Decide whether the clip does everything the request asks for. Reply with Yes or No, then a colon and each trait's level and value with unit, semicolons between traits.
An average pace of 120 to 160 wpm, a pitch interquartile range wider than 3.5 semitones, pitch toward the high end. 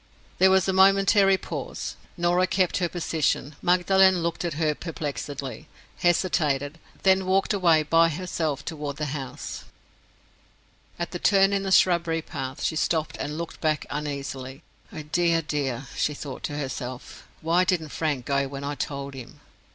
No: average, 150 wpm; average, 4.0 semitones; medium, 160 Hz